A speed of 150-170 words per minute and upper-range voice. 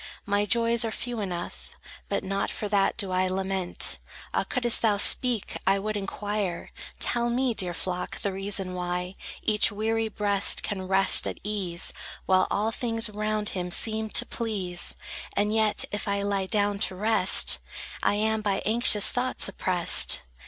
Yes: average, 160 wpm; high, 205 Hz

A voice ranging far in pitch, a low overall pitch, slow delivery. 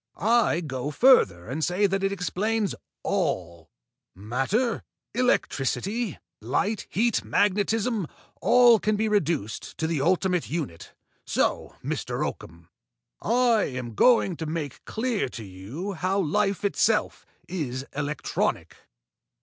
No: wide, 8.0 semitones; medium, 185 Hz; slow, 115 wpm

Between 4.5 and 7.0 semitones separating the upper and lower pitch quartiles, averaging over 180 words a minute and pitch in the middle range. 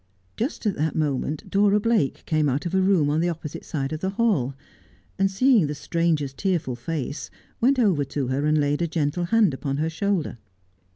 Yes: average, 5.2 semitones; average, 195 wpm; medium, 160 Hz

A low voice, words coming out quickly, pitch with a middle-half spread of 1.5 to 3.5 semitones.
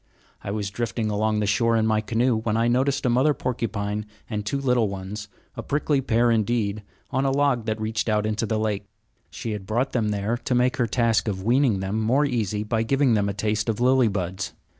Yes: low, 110 Hz; fast, 220 wpm; average, 2.7 semitones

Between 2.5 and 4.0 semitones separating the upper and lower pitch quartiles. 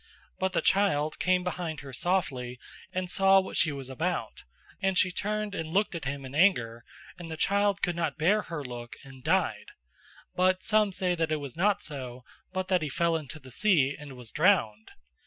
No: wide, 5.4 semitones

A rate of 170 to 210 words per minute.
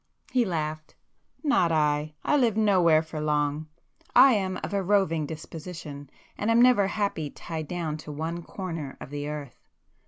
No: average, 160 wpm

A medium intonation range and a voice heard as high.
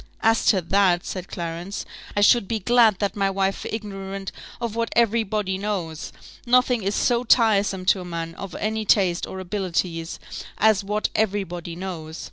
Yes: average, 3.0 semitones; high, 195 Hz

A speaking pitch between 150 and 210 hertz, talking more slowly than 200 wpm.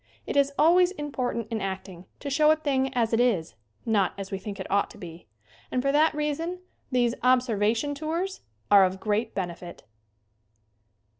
No: high, 245 Hz; average, 170 wpm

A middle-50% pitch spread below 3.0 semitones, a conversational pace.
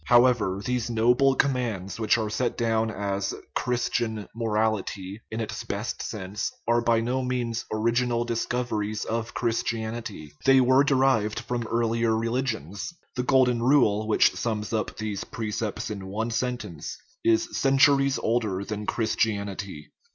Yes: narrow, 2.5 semitones; average, 145 wpm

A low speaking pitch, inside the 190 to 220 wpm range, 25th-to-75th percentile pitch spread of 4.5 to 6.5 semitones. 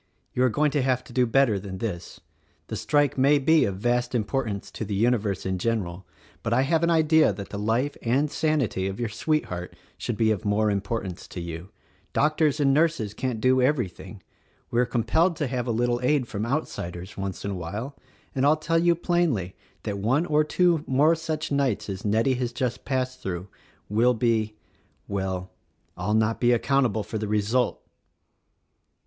Yes: low, 120 Hz; average, 195 wpm; wide, 5.5 semitones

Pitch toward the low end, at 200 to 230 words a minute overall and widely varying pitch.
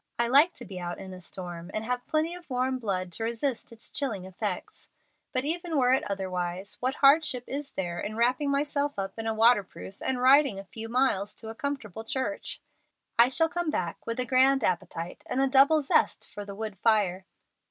No: high, 235 Hz; fast, 205 wpm; wide, 5.7 semitones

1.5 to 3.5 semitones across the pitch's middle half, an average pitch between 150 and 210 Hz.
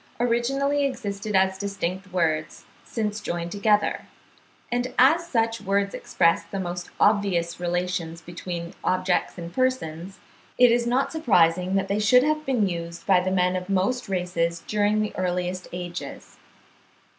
No: average, 4.3 semitones; high, 190 Hz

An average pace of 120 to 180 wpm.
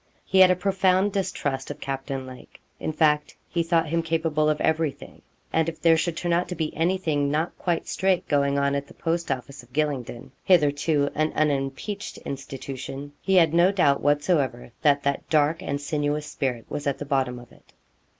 No: average, 190 wpm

